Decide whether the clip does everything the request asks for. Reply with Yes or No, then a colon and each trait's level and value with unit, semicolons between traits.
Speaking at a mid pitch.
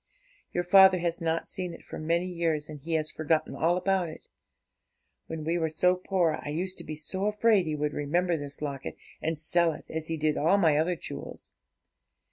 Yes: medium, 165 Hz